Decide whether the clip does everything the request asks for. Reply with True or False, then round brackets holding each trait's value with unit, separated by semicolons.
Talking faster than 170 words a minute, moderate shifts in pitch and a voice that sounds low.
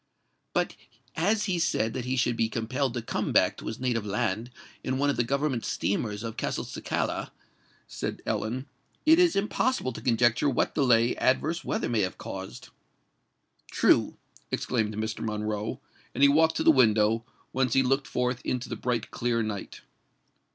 False (165 wpm; 3.5 semitones; 120 Hz)